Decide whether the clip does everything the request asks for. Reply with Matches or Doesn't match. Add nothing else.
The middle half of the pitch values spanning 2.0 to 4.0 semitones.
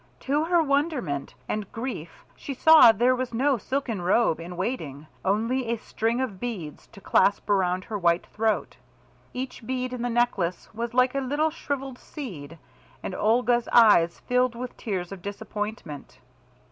Doesn't match